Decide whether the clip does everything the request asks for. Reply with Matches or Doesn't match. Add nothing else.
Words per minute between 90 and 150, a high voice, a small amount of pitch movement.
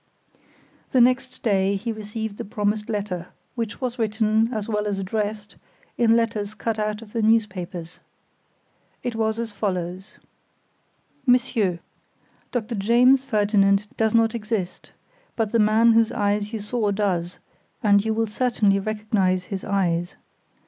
Matches